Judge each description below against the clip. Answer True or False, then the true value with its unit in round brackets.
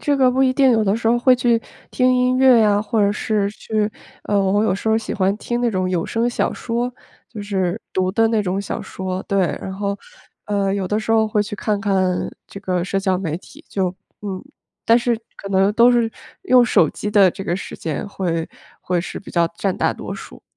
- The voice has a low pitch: False (205 Hz)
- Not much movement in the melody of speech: False (3.3 semitones)